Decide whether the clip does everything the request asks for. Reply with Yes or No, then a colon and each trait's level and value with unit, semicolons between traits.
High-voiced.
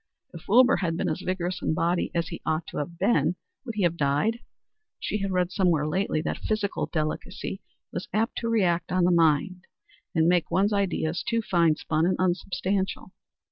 No: medium, 180 Hz